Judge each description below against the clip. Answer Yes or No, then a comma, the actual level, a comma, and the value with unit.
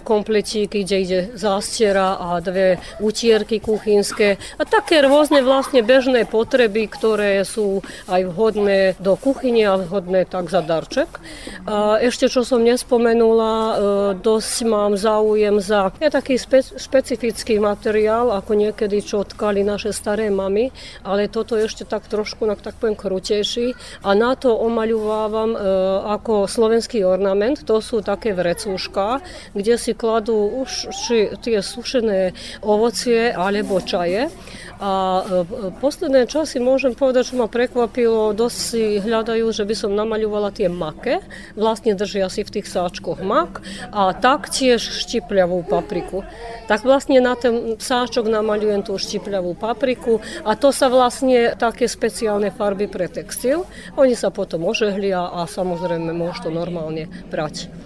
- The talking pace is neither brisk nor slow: Yes, average, 140 wpm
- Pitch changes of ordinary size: Yes, average, 3.2 semitones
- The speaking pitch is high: Yes, high, 215 Hz